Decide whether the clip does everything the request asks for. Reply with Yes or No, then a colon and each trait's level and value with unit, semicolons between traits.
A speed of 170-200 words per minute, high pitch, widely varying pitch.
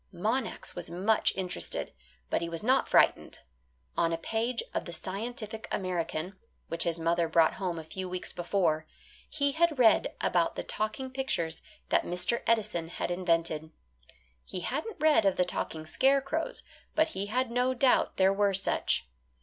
No: average, 160 wpm; high, 195 Hz; wide, 6.4 semitones